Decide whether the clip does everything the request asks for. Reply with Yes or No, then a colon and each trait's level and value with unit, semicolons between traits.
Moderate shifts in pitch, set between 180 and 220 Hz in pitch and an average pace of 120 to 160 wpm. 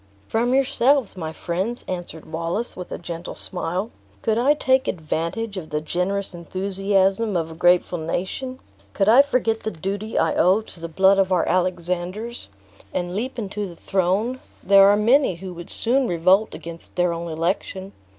No: average, 4.2 semitones; high, 190 Hz; average, 170 wpm